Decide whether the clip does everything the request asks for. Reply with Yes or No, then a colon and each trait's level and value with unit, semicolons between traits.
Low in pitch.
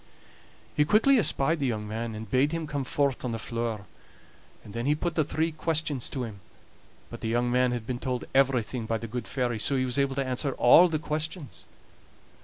Yes: low, 130 Hz